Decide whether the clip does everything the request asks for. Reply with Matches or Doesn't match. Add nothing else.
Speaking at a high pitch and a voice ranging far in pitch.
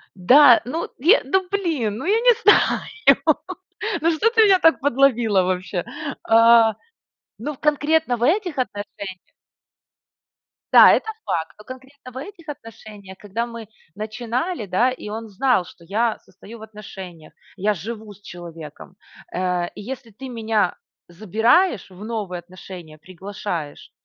Matches